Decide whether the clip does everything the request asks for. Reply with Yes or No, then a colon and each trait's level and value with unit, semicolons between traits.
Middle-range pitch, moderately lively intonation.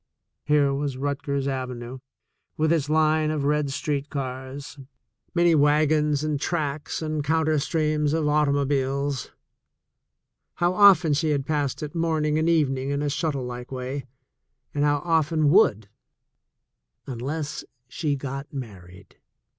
No: medium, 145 Hz; narrow, 2.2 semitones